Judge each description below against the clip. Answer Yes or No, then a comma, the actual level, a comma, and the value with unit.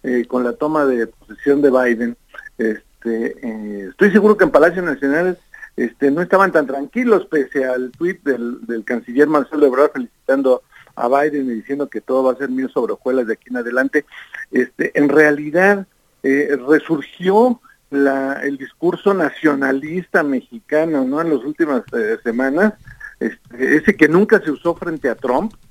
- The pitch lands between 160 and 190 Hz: No, medium, 145 Hz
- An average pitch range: No, wide, 6.1 semitones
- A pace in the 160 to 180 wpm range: Yes, average, 165 wpm